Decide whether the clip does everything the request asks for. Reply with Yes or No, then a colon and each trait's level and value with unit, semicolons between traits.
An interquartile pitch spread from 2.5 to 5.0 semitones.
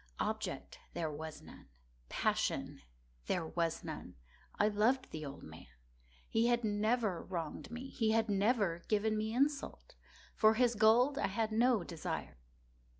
No: wide, 5.4 semitones